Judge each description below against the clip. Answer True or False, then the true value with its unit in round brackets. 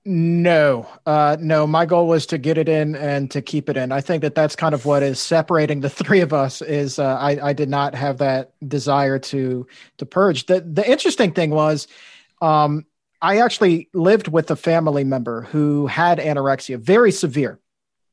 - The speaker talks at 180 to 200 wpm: True (190 wpm)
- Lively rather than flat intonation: False (2.9 semitones)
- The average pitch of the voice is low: False (150 Hz)